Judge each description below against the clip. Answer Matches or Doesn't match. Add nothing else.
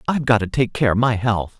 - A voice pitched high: Doesn't match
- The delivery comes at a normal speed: Doesn't match